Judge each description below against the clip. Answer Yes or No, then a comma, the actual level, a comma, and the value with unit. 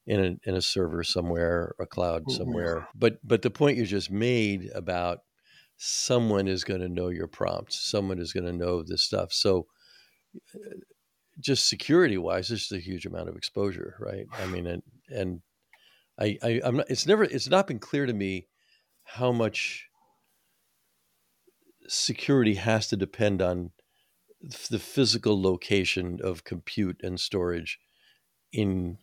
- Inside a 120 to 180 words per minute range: Yes, average, 155 wpm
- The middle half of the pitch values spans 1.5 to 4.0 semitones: No, average, 4.7 semitones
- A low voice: Yes, very low, 95 Hz